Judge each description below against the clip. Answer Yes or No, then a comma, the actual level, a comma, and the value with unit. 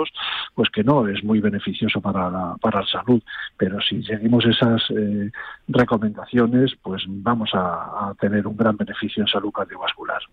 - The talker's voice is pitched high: No, low, 110 Hz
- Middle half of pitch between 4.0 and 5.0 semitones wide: No, narrow, 2.6 semitones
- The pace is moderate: Yes, average, 165 wpm